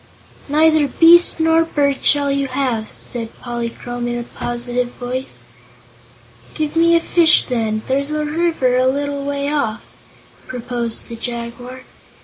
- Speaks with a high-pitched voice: Yes, very high, 260 Hz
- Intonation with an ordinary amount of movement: Yes, average, 3.8 semitones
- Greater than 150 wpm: No, slow, 135 wpm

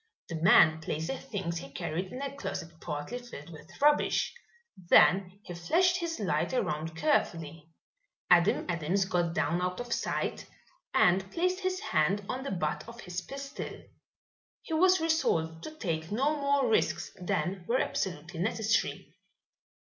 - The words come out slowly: No, average, 150 wpm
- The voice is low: No, high, 190 Hz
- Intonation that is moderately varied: No, wide, 8.3 semitones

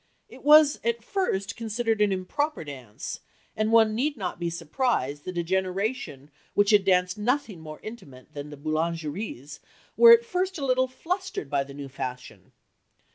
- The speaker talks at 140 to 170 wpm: Yes, average, 165 wpm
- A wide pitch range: Yes, wide, 8.7 semitones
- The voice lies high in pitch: Yes, high, 195 Hz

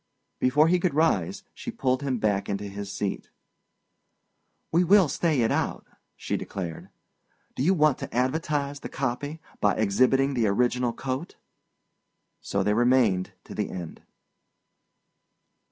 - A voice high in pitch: No, low, 125 Hz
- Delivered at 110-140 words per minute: Yes, slow, 135 wpm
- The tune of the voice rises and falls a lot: Yes, wide, 6.1 semitones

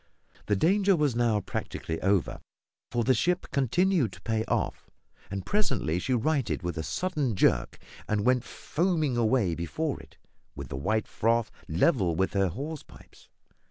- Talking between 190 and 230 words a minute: No, average, 160 wpm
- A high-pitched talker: No, low, 120 Hz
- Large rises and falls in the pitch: Yes, wide, 7.7 semitones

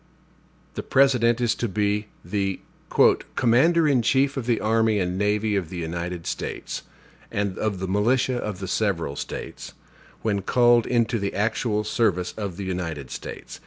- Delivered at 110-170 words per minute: Yes, average, 160 wpm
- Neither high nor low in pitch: No, low, 105 Hz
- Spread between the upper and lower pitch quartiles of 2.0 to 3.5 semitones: No, average, 3.9 semitones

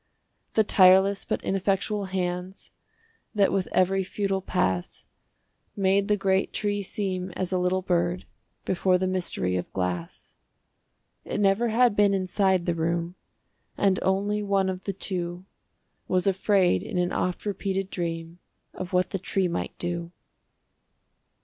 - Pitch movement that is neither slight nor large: No, narrow, 1.7 semitones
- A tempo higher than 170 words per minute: No, average, 140 wpm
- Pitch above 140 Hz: Yes, medium, 185 Hz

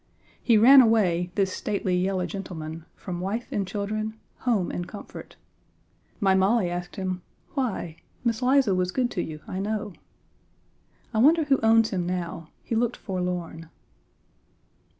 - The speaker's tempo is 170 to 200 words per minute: No, average, 145 wpm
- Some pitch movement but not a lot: Yes, average, 3.9 semitones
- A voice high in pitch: Yes, high, 195 Hz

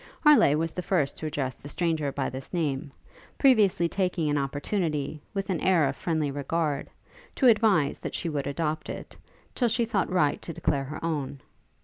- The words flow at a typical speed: Yes, average, 185 wpm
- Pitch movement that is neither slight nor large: Yes, average, 4.3 semitones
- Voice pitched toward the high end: No, medium, 155 Hz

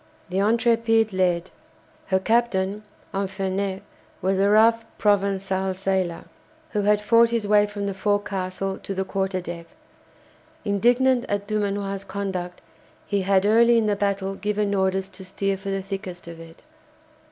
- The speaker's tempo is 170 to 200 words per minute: No, average, 145 wpm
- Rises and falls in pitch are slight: Yes, narrow, 1.7 semitones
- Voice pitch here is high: Yes, high, 195 Hz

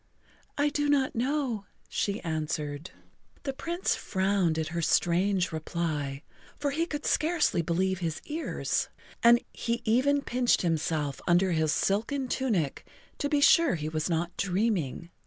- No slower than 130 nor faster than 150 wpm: Yes, average, 140 wpm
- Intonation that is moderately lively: No, wide, 8.7 semitones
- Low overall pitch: No, high, 195 Hz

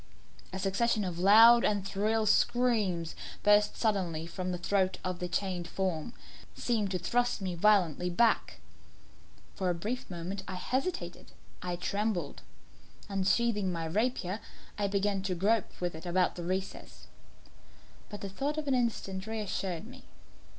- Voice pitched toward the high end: Yes, high, 195 Hz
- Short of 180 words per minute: Yes, average, 145 wpm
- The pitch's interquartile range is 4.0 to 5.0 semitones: No, average, 3.4 semitones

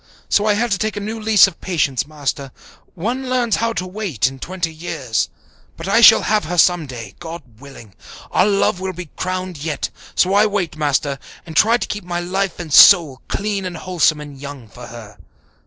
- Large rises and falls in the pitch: Yes, wide, 5.7 semitones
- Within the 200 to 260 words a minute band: Yes, fast, 205 wpm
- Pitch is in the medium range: Yes, medium, 175 Hz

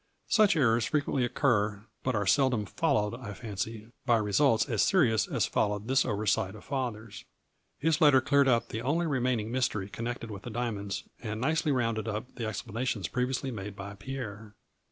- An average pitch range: Yes, average, 3.8 semitones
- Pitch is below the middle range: Yes, low, 115 Hz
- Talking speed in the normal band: Yes, average, 170 wpm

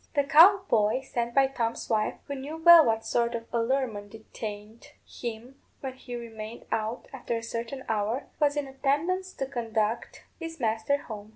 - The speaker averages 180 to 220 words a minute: No, average, 170 wpm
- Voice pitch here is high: Yes, high, 240 Hz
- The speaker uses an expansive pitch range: No, average, 3.8 semitones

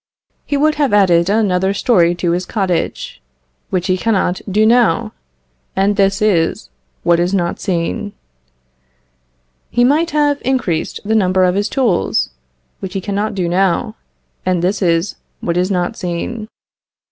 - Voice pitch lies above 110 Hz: Yes, high, 190 Hz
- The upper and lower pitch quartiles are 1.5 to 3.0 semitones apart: No, average, 3.5 semitones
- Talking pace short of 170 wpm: Yes, average, 145 wpm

